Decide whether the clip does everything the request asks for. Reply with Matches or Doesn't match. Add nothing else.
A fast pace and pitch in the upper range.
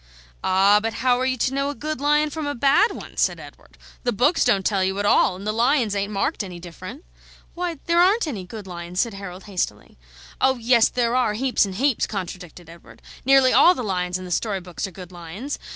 Matches